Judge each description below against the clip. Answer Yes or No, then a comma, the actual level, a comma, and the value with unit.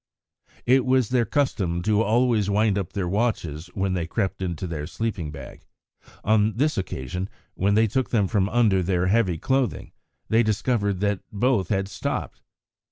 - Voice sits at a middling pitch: No, low, 100 Hz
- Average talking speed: Yes, average, 165 wpm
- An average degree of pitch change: Yes, average, 3.8 semitones